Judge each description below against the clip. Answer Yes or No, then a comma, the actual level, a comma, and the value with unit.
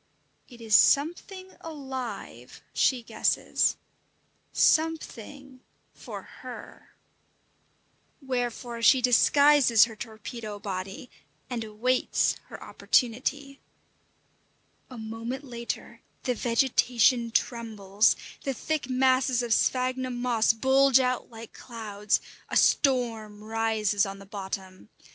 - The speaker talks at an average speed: No, slow, 100 wpm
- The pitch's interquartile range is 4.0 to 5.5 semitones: No, average, 3.1 semitones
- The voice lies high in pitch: Yes, high, 240 Hz